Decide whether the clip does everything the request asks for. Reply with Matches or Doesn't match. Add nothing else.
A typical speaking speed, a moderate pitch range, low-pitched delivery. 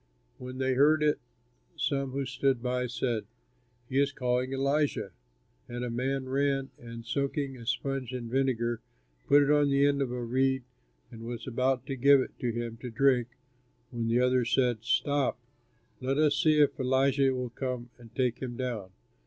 Doesn't match